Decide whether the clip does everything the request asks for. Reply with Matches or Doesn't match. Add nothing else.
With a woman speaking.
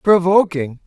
Doesn't match